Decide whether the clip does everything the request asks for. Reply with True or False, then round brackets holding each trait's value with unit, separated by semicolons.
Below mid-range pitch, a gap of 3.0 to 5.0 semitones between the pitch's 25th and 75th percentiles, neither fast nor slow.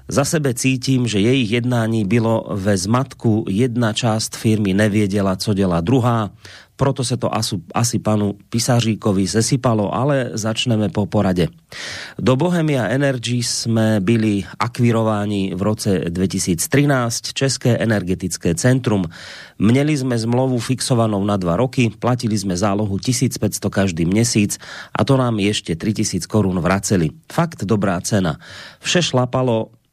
True (110 Hz; 3.7 semitones; 130 wpm)